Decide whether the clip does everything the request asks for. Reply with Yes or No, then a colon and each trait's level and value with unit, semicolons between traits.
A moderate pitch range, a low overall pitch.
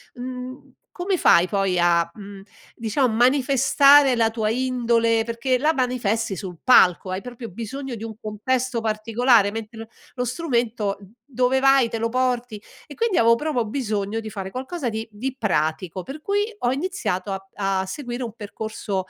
No: average, 3.6 semitones; high, 230 Hz